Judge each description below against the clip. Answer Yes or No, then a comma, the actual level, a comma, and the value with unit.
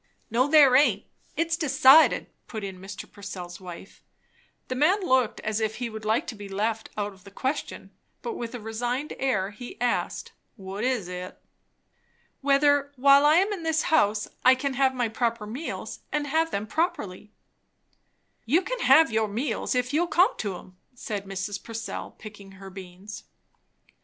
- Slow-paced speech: No, average, 170 wpm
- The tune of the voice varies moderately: No, wide, 5.7 semitones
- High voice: Yes, high, 235 Hz